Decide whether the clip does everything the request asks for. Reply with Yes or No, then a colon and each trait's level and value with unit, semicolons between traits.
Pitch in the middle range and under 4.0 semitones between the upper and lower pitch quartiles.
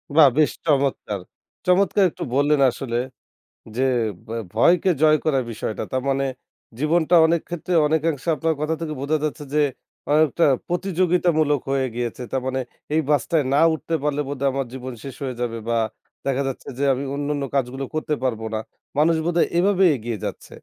Yes: medium, 145 Hz; average, 3.5 semitones